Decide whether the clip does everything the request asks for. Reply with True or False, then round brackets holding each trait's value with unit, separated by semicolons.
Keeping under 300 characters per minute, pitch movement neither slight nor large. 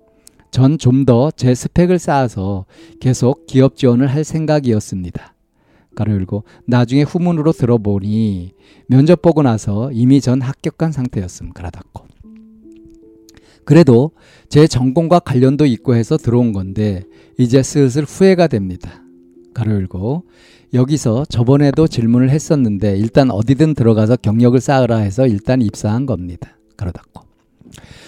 True (290 characters per minute; 5.0 semitones)